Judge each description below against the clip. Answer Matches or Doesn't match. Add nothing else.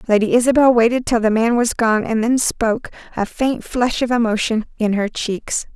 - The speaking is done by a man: Doesn't match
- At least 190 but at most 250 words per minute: Matches